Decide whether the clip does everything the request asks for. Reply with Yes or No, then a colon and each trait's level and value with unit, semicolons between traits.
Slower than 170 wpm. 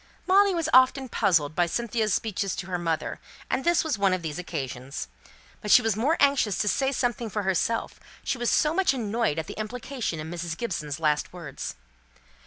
No: average, 195 wpm